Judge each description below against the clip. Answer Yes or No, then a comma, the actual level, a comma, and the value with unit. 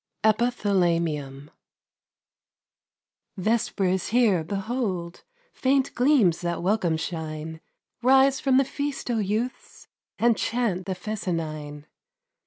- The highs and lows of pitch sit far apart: Yes, wide, 6.3 semitones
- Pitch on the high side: Yes, high, 195 Hz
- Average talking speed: No, slow, 95 wpm